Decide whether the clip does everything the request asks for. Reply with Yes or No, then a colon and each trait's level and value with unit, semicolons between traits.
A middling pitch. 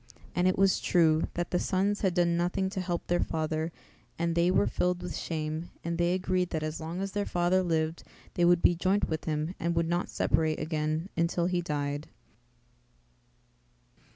Yes: medium, 170 Hz